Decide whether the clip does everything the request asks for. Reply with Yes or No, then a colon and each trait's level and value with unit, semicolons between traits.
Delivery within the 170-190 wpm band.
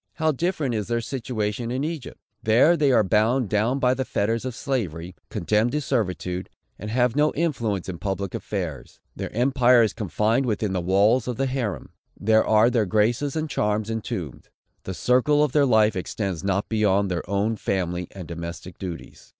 Yes: average, 180 wpm